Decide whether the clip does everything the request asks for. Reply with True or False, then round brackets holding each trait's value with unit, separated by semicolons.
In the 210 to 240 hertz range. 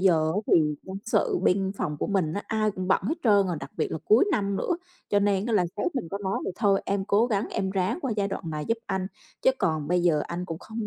False (195 Hz)